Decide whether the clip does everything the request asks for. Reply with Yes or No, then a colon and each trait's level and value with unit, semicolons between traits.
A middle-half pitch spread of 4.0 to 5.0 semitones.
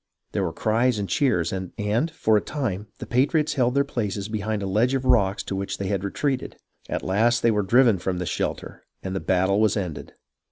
Yes: average, 4.4 semitones